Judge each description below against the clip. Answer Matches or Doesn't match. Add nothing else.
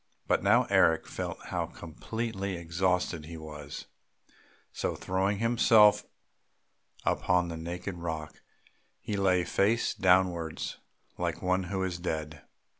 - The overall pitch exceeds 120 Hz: Doesn't match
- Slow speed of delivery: Matches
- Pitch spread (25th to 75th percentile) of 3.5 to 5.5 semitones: Doesn't match